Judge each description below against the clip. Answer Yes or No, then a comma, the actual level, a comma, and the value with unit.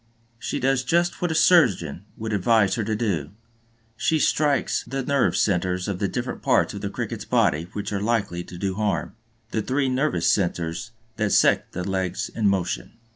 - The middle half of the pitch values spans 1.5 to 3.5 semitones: No, wide, 5.6 semitones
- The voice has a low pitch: Yes, low, 105 Hz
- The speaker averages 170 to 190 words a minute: Yes, average, 180 wpm